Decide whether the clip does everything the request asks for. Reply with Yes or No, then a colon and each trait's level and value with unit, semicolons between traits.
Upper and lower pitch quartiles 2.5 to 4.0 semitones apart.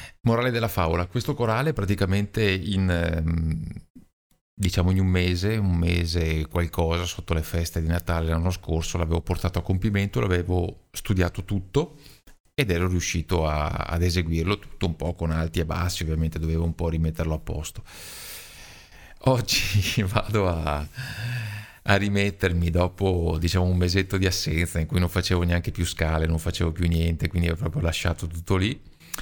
Yes: average, 3.0 semitones